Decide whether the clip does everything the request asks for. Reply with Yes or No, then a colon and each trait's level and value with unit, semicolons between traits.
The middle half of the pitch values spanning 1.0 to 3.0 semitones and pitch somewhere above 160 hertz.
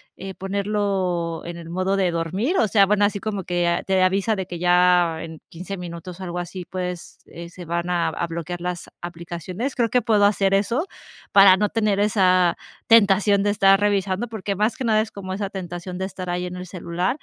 Yes: narrow, 2.5 semitones; medium, 185 Hz